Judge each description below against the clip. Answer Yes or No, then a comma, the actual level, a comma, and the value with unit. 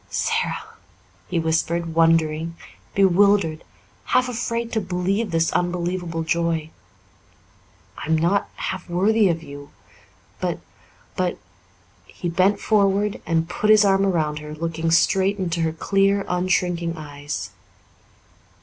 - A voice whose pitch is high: No, medium, 175 Hz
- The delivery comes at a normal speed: No, slow, 115 wpm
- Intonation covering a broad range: No, average, 3.2 semitones